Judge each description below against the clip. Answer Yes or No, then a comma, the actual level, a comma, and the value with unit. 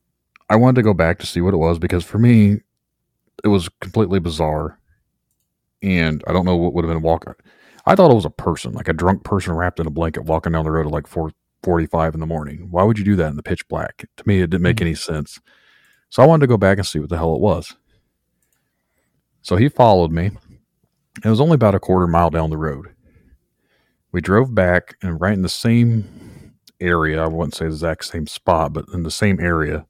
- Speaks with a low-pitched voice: Yes, very low, 90 Hz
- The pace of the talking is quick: Yes, fast, 235 wpm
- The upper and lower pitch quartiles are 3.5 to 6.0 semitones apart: Yes, average, 3.8 semitones